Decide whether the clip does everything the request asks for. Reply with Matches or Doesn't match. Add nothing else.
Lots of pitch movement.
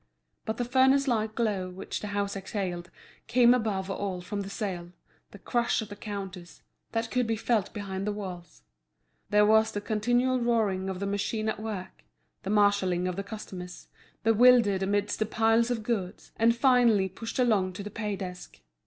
Doesn't match